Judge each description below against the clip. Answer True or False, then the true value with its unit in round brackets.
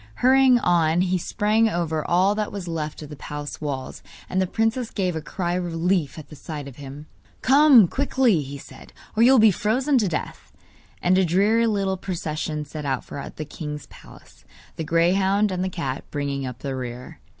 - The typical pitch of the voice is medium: True (175 Hz)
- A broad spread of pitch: True (5.7 semitones)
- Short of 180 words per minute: False (195 wpm)